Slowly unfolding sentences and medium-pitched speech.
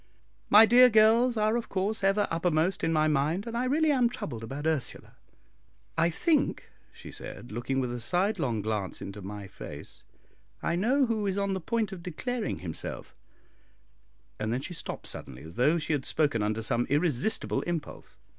No: average, 175 wpm; medium, 170 Hz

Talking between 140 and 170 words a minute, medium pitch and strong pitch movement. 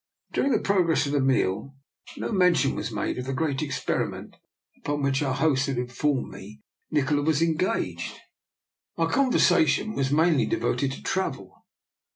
No: average, 165 wpm; medium, 145 Hz; average, 3.6 semitones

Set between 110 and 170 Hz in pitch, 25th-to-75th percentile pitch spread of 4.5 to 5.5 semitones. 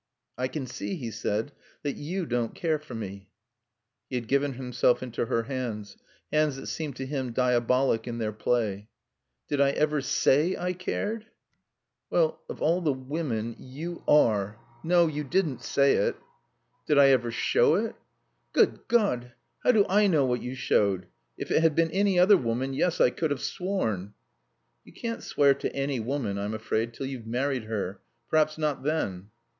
Yes: low, 135 Hz; average, 5.1 semitones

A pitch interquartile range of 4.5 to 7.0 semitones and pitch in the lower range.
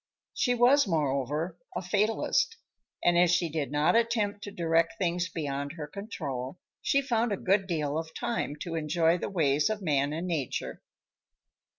No: average, 5.3 semitones; medium, 170 Hz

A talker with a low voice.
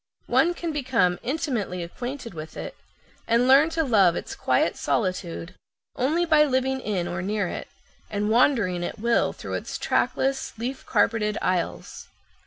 No: high, 230 Hz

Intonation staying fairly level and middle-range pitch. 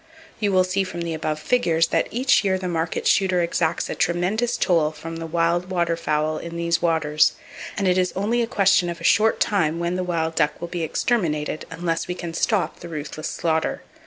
Yes: narrow, 2.3 semitones; medium, 170 Hz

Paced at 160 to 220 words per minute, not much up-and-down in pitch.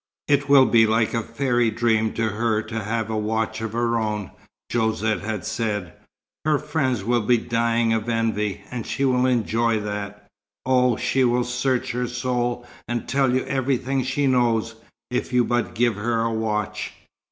Yes: average, 175 wpm; narrow, 2.0 semitones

